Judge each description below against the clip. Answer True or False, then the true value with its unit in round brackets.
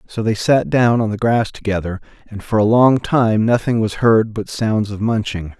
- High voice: False (110 Hz)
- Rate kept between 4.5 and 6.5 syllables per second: True (4.6 syllables/s)